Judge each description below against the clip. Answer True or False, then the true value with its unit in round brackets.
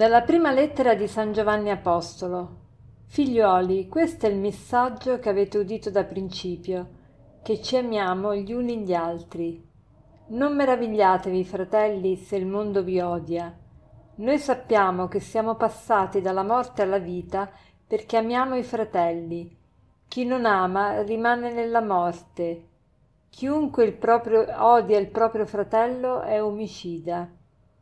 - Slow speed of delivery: False (130 wpm)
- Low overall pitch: False (205 Hz)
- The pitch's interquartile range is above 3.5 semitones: True (4.1 semitones)